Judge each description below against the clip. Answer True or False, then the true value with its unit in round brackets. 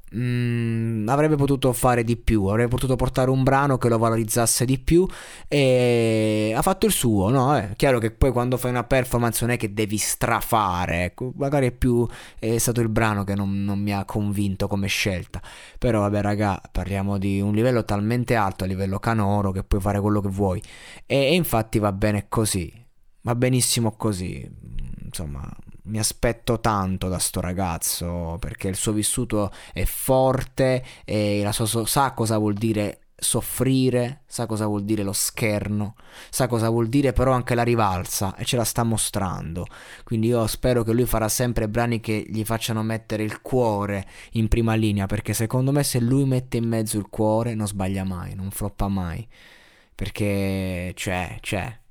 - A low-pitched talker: True (110 Hz)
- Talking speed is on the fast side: True (180 wpm)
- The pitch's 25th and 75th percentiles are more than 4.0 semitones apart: False (3.2 semitones)